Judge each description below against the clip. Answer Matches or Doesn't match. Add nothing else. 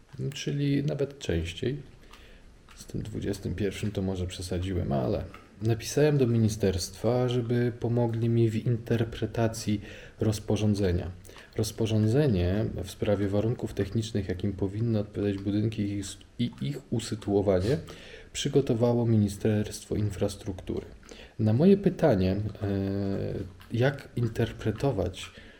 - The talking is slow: Matches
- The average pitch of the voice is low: Matches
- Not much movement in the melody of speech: Doesn't match